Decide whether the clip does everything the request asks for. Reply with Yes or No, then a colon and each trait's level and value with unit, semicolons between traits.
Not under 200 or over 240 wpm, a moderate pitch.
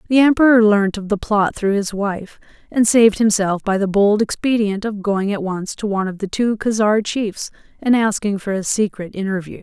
No: fast, 205 wpm; high, 210 Hz